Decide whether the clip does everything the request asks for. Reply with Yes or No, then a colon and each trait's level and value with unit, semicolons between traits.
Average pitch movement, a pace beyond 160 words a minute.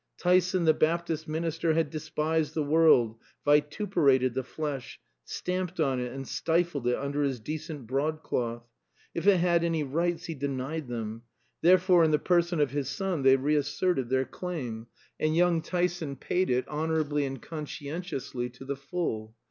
No: average, 4.1 semitones; average, 155 wpm